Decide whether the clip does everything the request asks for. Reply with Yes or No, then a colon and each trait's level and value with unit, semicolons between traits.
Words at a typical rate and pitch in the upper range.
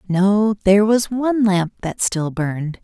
Yes: average, 170 wpm; high, 200 Hz